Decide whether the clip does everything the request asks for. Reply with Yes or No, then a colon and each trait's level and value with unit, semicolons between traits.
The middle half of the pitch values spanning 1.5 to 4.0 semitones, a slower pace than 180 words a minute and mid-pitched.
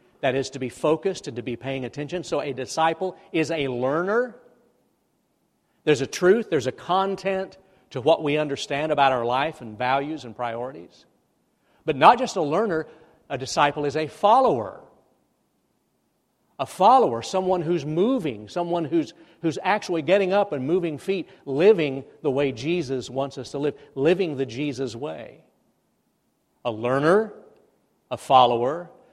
No: average, 4.7 semitones; average, 150 wpm; medium, 155 Hz